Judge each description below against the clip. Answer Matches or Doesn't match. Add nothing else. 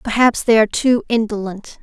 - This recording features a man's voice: Doesn't match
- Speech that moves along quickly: Doesn't match